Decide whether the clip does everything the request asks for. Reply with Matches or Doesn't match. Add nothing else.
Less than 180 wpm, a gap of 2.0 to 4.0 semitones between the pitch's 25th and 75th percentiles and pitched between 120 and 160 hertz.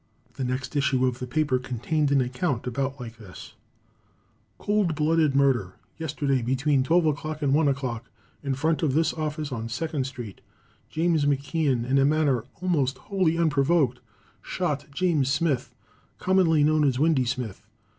Matches